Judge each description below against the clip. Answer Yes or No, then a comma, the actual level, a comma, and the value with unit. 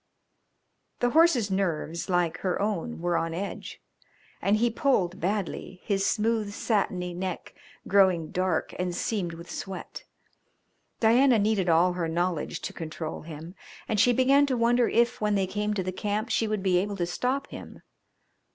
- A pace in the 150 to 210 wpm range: Yes, average, 160 wpm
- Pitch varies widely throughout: No, average, 3.9 semitones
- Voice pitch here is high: Yes, high, 195 Hz